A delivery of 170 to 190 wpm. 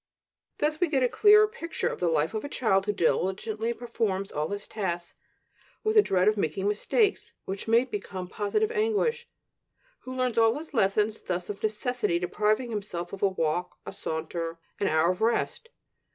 Yes: average, 180 wpm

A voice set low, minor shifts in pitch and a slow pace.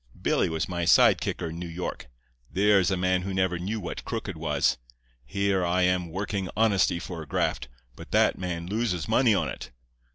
No: very low, 90 Hz; narrow, 2.2 semitones; average, 195 wpm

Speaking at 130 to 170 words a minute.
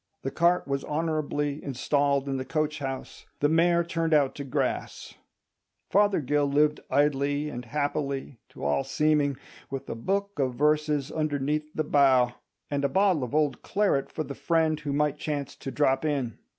Yes: average, 165 wpm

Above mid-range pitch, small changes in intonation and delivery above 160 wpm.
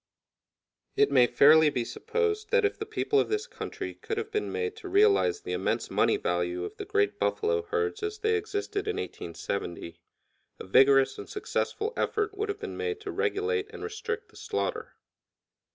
Yes: very high, 425 Hz; narrow, 1.5 semitones; average, 180 wpm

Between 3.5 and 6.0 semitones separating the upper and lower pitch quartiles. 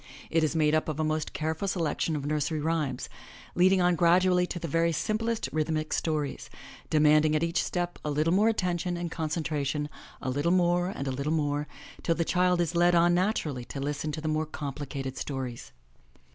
No: average, 2.8 semitones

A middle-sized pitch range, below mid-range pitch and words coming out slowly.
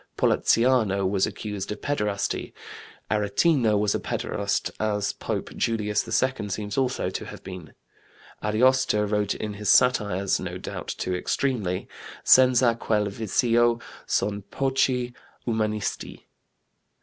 Yes: average, 3.3 semitones; low, 105 Hz; slow, 115 wpm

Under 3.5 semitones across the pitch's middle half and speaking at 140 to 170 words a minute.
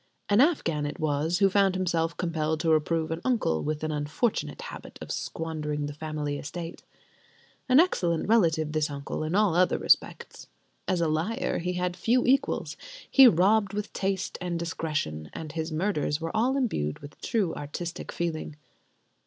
No: average, 4.0 semitones; average, 165 wpm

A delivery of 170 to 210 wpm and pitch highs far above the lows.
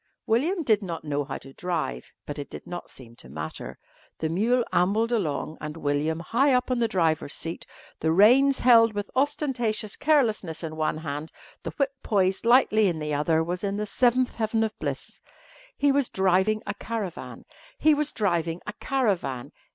Yes: average, 180 wpm; wide, 6.9 semitones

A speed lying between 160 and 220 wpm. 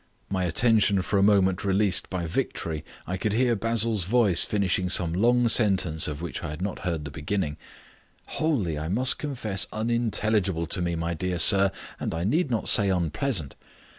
Yes: average, 180 wpm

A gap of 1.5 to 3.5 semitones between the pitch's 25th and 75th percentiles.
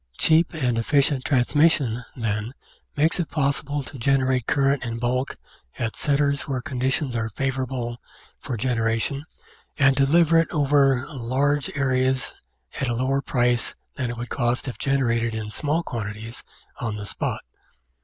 Yes: average, 3.1 semitones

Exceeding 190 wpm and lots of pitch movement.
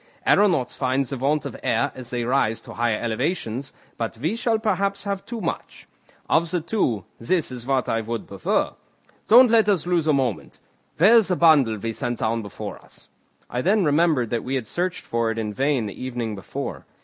Yes: average, 200 wpm; wide, 7.4 semitones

